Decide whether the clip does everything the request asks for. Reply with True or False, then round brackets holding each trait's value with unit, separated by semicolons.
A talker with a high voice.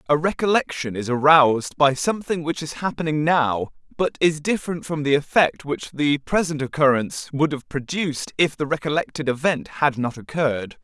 False (150 Hz)